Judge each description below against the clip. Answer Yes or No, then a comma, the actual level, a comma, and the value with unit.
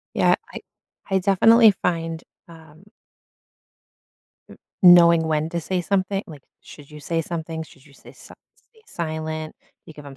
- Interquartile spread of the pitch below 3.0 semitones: Yes, narrow, 2.4 semitones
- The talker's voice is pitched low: No, medium, 165 Hz